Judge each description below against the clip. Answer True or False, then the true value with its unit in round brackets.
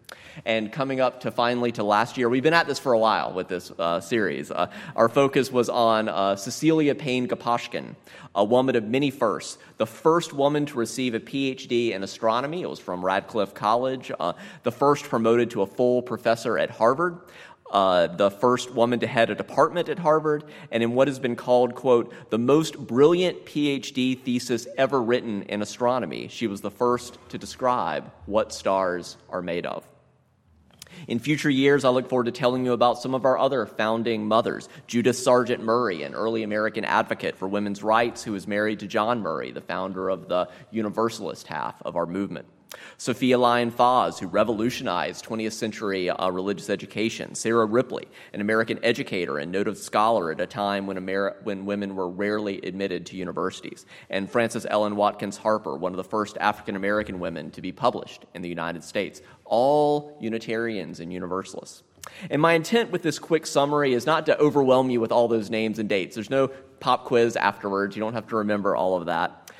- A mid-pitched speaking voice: False (115 Hz)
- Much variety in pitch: False (3.8 semitones)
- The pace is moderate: True (190 wpm)